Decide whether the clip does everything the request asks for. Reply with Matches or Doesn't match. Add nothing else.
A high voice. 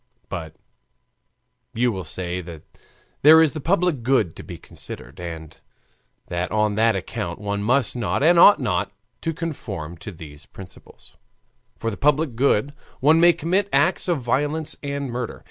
Doesn't match